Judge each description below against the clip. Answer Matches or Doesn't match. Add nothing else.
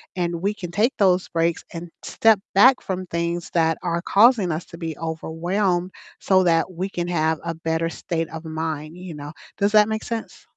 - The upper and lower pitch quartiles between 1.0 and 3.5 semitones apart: Matches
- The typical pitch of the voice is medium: Matches